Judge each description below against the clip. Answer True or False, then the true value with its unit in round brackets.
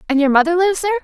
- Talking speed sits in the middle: False (290 wpm)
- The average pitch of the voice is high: True (335 Hz)